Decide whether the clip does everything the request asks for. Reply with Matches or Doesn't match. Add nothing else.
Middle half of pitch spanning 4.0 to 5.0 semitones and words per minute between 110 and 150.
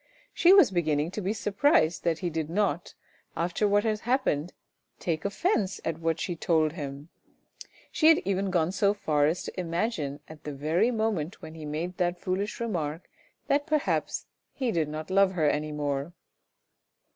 Doesn't match